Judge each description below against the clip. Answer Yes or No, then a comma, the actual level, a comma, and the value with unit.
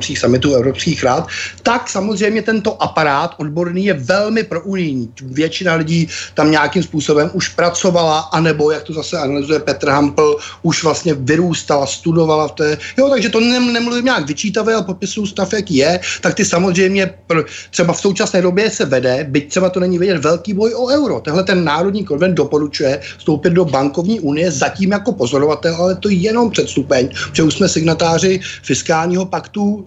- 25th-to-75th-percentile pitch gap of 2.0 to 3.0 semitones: No, average, 4.5 semitones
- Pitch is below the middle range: No, medium, 170 Hz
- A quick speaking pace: Yes, fast, 175 wpm